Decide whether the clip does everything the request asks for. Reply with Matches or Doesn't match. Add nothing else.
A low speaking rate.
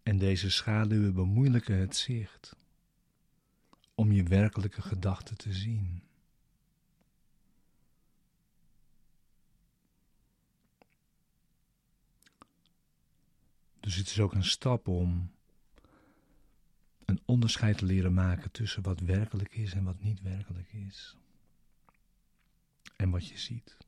Matches